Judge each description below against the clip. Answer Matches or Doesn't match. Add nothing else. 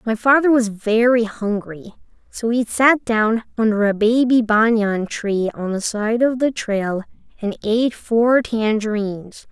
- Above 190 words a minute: Doesn't match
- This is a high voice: Matches